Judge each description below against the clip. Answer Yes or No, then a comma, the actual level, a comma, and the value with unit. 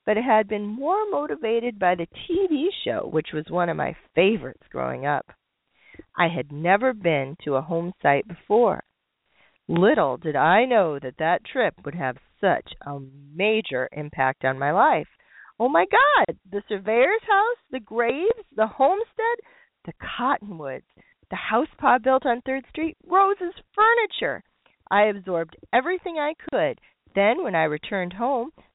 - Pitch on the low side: No, high, 220 Hz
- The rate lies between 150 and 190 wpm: Yes, average, 155 wpm